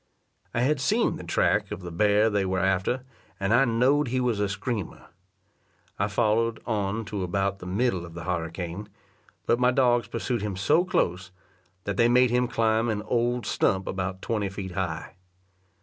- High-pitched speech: No, low, 105 Hz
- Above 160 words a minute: Yes, average, 180 wpm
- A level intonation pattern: No, average, 4.2 semitones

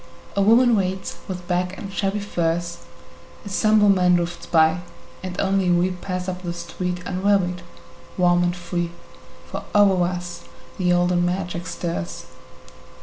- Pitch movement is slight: Yes, narrow, 1.6 semitones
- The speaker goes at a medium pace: Yes, average, 145 wpm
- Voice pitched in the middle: Yes, medium, 180 Hz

